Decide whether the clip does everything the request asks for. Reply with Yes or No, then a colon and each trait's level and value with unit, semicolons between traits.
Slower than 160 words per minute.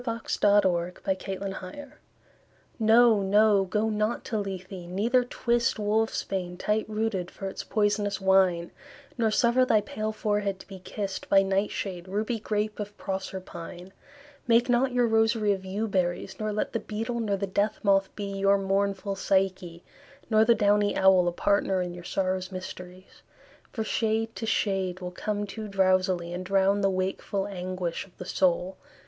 No: average, 165 wpm